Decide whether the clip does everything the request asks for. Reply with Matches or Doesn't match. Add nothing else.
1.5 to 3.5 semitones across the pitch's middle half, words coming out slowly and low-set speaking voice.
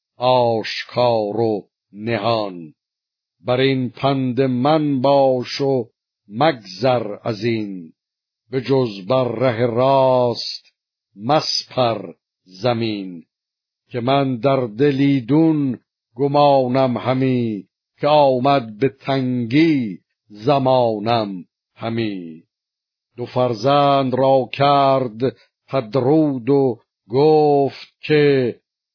Matches